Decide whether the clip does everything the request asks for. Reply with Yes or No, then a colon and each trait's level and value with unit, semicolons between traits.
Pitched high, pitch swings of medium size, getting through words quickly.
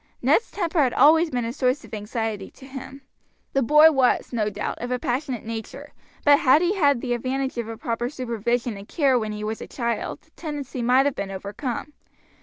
Yes: very high, 250 Hz; average, 3.7 semitones; fast, 210 wpm